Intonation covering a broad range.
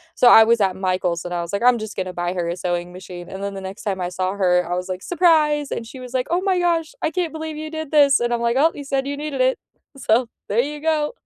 Yes: wide, 8.3 semitones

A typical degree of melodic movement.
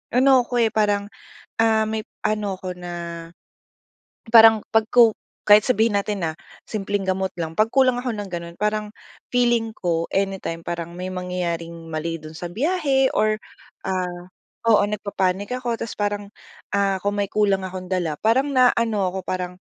Yes: average, 3.6 semitones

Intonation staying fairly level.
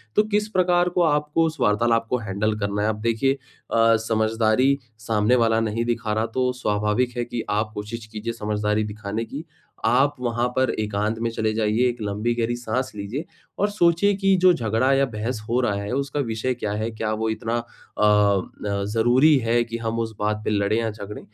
No: average, 3.0 semitones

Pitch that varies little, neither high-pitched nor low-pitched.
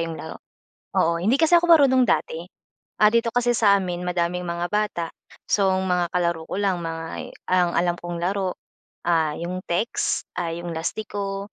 No: average, 3.4 semitones; medium, 180 Hz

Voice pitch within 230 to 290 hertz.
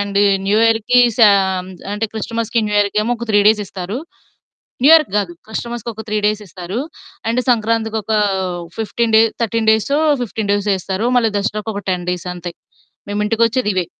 No: high, 215 Hz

